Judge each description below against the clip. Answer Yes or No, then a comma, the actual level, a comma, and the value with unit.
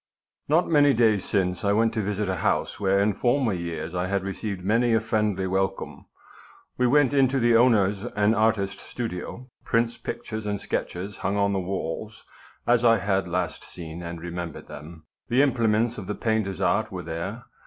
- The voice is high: No, low, 105 Hz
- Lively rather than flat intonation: No, average, 3.7 semitones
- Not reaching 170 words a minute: No, average, 180 wpm